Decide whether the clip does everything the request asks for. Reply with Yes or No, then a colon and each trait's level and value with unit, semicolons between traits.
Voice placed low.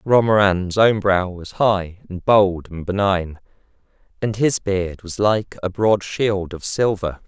Yes: very low, 95 Hz